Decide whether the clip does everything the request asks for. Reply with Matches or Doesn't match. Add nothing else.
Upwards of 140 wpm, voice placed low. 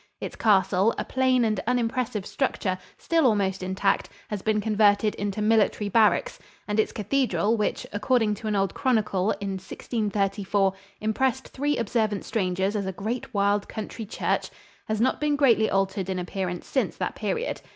Doesn't match